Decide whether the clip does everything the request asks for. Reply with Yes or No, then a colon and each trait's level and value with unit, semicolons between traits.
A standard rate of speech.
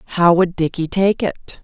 Yes: average, 185 wpm